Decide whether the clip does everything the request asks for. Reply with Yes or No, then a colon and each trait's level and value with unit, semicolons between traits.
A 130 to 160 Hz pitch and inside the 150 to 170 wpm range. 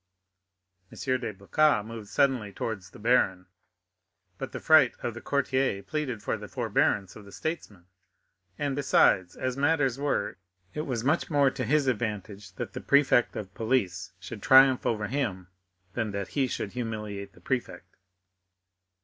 No: low, 120 Hz; average, 155 wpm